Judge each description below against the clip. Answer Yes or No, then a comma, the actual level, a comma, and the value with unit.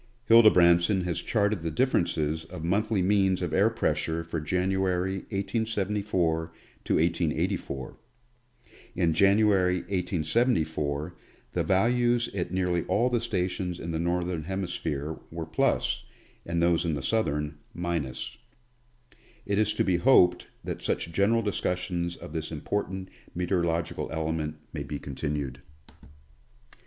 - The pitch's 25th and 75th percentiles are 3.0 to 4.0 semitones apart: Yes, average, 3.5 semitones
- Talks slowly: Yes, slow, 125 wpm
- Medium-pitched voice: No, very low, 90 Hz